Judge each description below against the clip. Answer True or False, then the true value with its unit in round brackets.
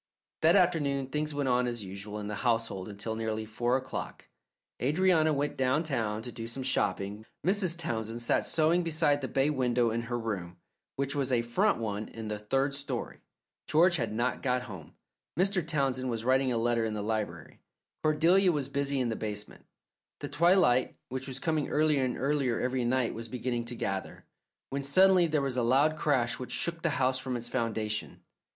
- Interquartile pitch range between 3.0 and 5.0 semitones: True (4.6 semitones)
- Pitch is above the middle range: False (130 Hz)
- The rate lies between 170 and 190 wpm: True (185 wpm)